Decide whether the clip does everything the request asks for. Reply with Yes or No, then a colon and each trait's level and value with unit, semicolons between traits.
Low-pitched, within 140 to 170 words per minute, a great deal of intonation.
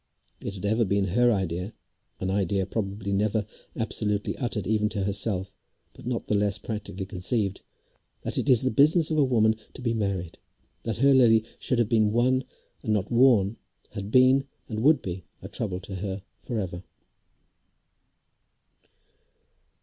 No: low, 105 Hz; average, 160 wpm; average, 3.4 semitones